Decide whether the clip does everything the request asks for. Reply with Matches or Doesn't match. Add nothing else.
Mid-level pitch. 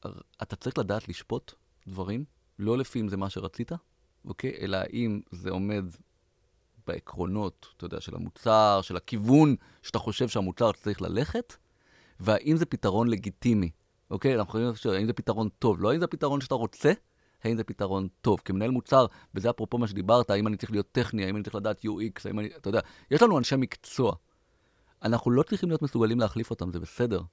Doesn't match